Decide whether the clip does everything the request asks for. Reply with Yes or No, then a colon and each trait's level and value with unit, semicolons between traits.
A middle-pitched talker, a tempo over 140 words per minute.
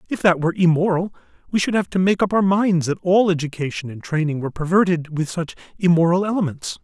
Yes: medium, 175 Hz; average, 200 wpm